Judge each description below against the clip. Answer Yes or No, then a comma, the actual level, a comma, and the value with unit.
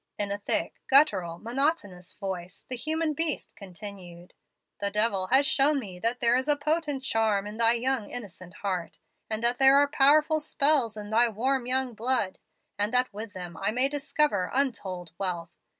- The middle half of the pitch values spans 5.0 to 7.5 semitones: Yes, wide, 5.5 semitones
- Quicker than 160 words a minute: Yes, average, 170 wpm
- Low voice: No, high, 230 Hz